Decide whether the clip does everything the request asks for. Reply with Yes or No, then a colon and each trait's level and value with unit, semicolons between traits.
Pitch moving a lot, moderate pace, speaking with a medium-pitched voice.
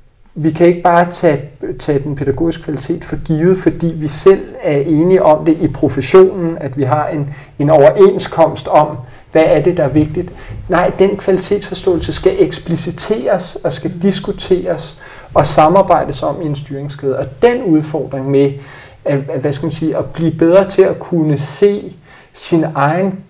No: average, 3.9 semitones; average, 160 wpm; medium, 160 Hz